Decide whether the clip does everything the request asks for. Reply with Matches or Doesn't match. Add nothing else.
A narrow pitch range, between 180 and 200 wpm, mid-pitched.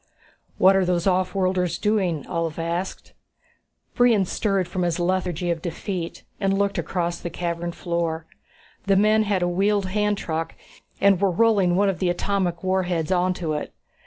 Doesn't match